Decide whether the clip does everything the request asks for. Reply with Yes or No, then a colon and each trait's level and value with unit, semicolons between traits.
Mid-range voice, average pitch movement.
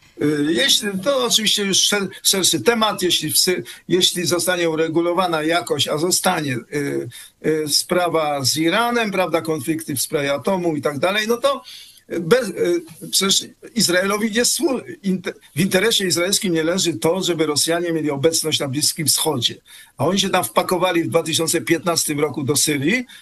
Yes: medium, 170 Hz; average, 3.3 semitones